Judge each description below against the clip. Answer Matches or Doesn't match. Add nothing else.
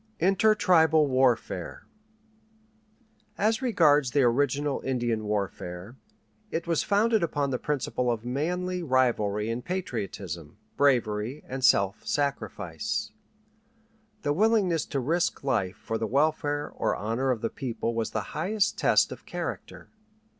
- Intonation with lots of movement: Matches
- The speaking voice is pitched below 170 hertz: Matches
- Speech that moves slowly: Matches